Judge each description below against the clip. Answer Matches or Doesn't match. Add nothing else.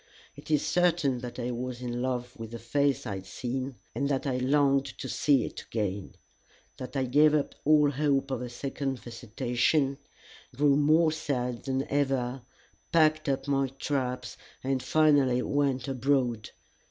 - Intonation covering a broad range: Doesn't match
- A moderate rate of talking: Matches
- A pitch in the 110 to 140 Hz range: Matches